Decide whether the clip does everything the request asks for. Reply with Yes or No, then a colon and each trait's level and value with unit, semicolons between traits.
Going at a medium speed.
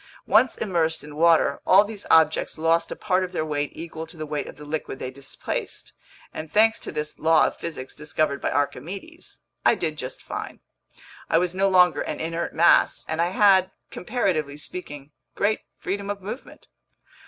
Yes: average, 180 wpm